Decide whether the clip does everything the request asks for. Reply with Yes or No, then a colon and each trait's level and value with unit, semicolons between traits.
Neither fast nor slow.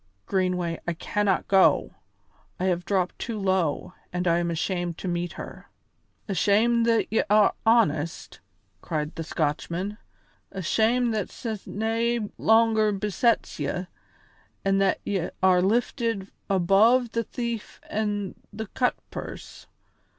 No: slow, 125 wpm